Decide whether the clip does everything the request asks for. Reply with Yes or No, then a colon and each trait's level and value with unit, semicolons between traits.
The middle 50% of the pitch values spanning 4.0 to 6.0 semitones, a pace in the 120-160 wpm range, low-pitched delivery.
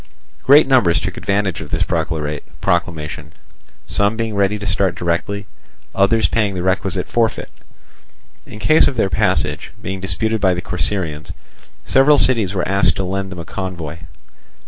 No: average, 3.5 semitones; average, 150 wpm; very low, 95 Hz